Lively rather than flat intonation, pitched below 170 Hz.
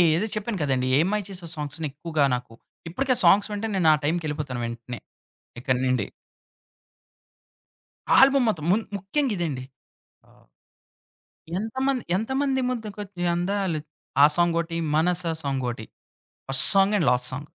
No: wide, 6.5 semitones; medium, 175 Hz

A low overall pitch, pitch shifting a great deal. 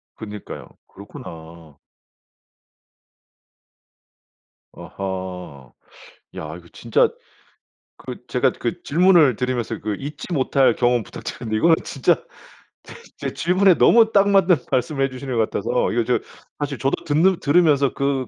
Yes: low, 130 Hz; wide, 6.7 semitones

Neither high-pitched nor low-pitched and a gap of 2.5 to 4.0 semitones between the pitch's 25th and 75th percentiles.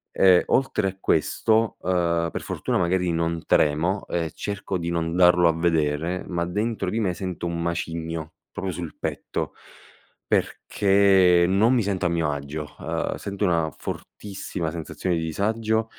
No: very low, 90 Hz; average, 2.9 semitones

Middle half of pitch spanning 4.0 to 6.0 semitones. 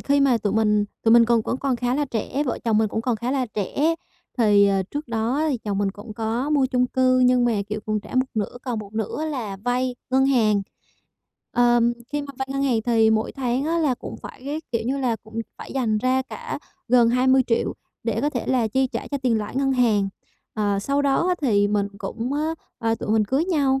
No: average, 3.5 semitones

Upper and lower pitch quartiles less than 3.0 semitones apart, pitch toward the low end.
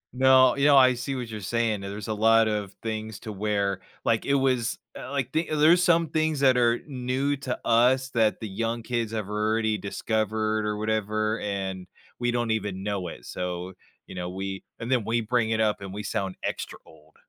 No: average, 3.3 semitones; low, 110 Hz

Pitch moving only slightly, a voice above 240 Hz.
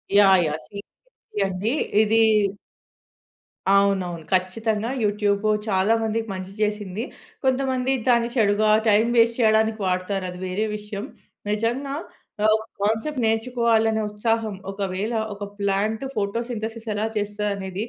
No: narrow, 2.1 semitones; high, 215 Hz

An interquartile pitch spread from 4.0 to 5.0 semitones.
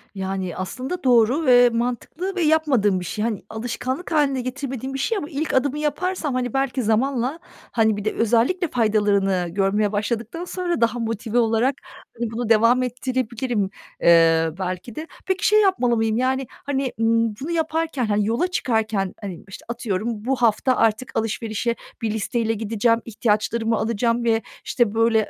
No: average, 3.6 semitones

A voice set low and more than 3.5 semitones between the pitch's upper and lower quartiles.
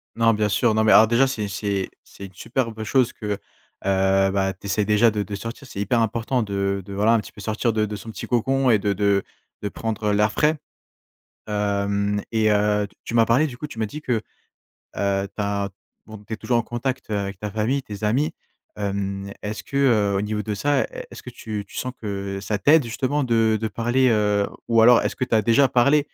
No: low, 110 Hz; average, 2.7 semitones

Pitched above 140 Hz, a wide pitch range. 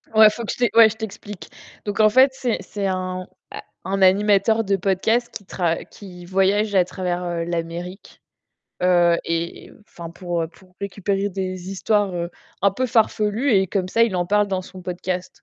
No: high, 190 Hz; average, 2.7 semitones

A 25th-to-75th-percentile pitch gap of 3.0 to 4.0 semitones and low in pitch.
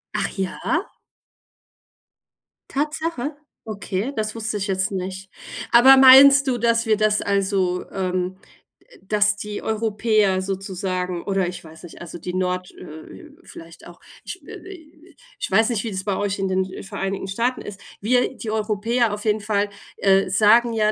No: average, 3.4 semitones; high, 205 Hz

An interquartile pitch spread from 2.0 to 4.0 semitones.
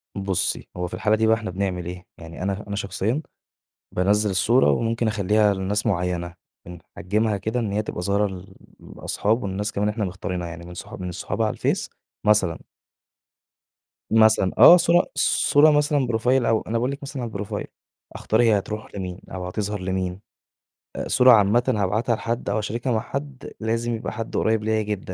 Yes: average, 3.3 semitones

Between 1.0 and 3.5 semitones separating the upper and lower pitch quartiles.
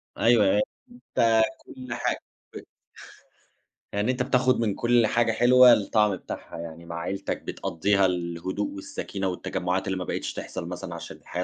No: average, 4.7 semitones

